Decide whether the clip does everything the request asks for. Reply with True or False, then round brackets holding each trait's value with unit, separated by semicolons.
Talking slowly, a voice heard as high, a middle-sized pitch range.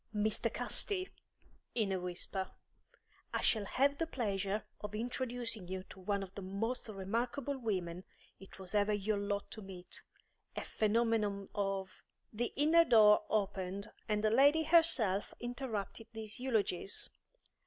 False (145 wpm; 210 Hz; 3.6 semitones)